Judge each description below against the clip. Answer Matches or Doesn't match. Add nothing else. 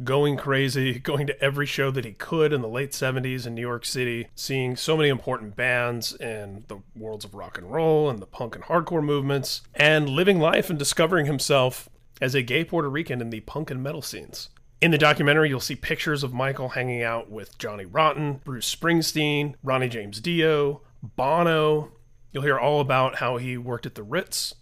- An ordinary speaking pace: Matches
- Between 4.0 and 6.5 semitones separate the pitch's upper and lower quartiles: Doesn't match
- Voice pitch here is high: Doesn't match